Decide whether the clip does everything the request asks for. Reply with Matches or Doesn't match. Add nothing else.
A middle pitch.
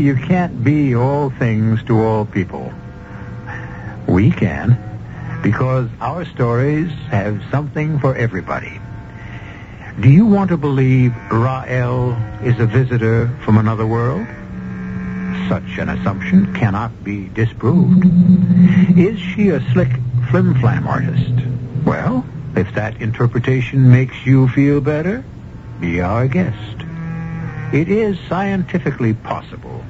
Doesn't match